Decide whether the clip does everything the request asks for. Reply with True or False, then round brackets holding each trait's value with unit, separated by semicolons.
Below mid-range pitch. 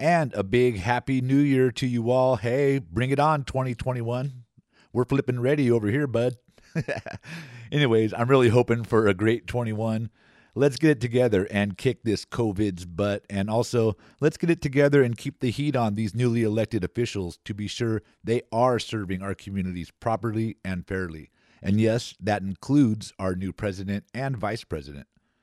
True (115 Hz)